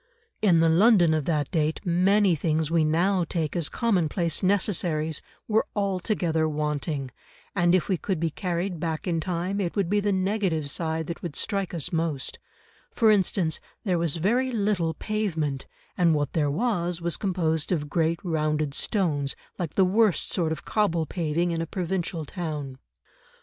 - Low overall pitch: No, medium, 170 Hz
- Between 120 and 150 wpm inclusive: No, average, 165 wpm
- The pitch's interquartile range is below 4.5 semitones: Yes, average, 3.4 semitones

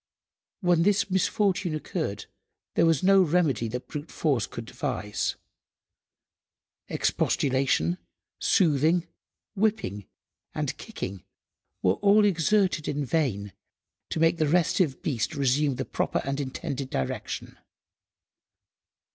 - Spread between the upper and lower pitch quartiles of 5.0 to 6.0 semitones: Yes, wide, 5.4 semitones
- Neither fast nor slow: No, slow, 105 wpm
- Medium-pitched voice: Yes, medium, 155 Hz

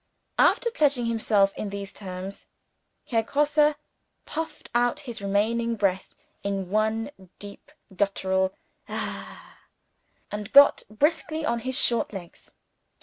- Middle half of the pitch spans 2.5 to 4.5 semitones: No, wide, 5.4 semitones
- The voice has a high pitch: Yes, high, 220 Hz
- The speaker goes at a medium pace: No, slow, 115 wpm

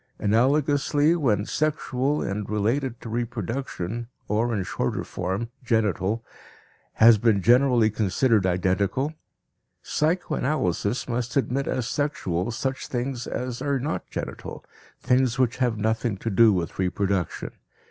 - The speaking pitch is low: Yes, low, 115 Hz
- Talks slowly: Yes, slow, 120 wpm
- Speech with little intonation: No, average, 4.2 semitones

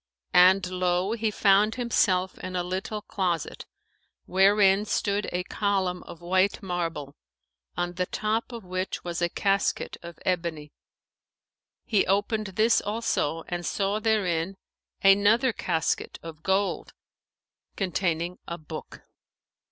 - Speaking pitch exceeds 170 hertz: Yes, medium, 185 Hz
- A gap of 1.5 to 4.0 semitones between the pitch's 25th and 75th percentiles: Yes, narrow, 2.6 semitones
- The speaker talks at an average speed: No, slow, 120 wpm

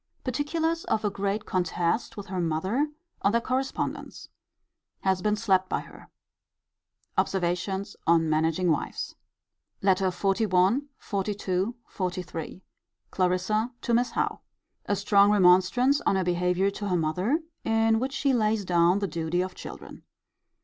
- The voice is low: No, high, 195 Hz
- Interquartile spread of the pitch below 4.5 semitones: Yes, average, 3.7 semitones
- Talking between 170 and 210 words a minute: No, slow, 135 wpm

